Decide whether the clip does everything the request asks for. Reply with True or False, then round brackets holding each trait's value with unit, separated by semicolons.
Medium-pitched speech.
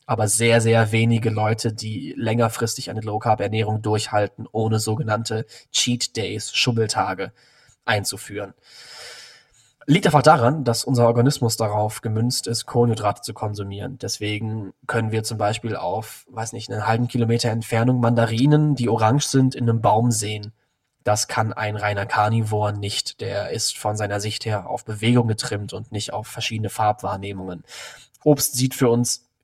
False (115 Hz)